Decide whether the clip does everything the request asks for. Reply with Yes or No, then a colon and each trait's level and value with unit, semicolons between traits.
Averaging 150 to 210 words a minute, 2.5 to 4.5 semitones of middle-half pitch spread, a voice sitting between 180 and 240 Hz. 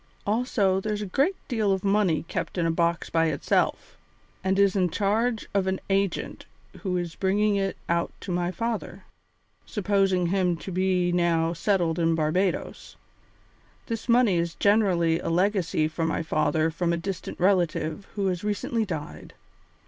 Yes: average, 160 wpm; average, 3.1 semitones; medium, 185 Hz